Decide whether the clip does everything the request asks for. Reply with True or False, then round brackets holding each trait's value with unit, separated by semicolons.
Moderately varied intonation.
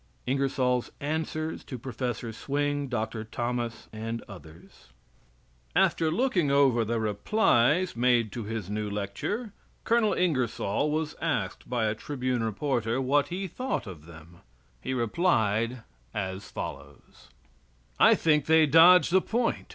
False (6.0 semitones)